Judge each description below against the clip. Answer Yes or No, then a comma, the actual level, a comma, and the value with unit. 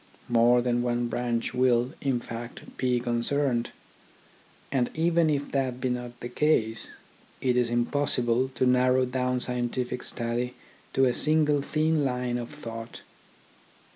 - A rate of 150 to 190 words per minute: No, average, 140 wpm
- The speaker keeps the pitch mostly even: Yes, narrow, 1.9 semitones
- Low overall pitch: Yes, low, 125 Hz